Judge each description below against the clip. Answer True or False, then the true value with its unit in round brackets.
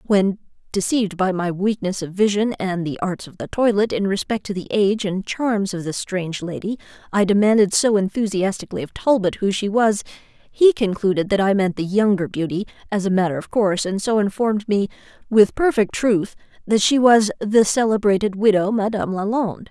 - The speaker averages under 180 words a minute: False (185 wpm)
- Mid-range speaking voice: False (200 Hz)